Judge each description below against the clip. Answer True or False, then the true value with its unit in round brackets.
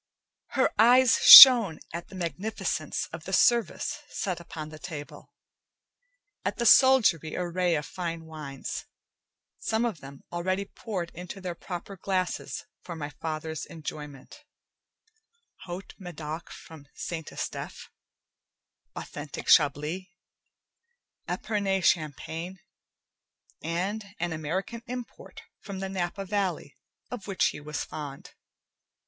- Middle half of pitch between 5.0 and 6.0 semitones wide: False (4.1 semitones)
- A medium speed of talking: False (115 wpm)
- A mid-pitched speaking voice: True (175 Hz)